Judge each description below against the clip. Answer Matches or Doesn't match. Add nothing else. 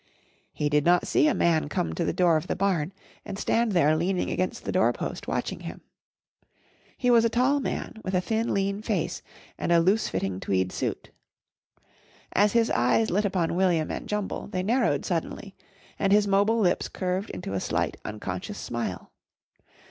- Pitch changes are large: Doesn't match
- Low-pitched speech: Doesn't match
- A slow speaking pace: Doesn't match